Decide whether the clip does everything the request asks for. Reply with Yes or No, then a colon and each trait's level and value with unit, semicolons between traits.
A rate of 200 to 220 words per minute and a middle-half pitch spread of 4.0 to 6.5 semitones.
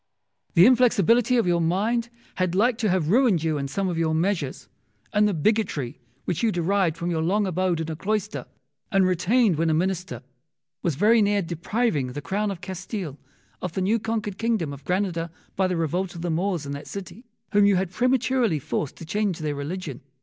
Yes: fast, 205 wpm; average, 4.3 semitones